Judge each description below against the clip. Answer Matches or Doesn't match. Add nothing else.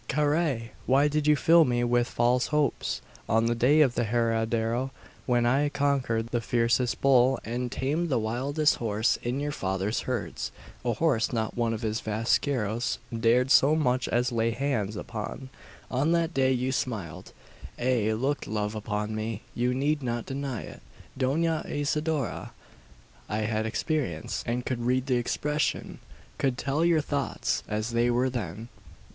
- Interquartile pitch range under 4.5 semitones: Matches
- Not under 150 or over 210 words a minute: Matches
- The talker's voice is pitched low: Matches